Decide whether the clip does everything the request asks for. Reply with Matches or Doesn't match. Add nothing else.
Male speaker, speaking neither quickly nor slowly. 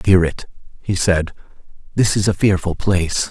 Matches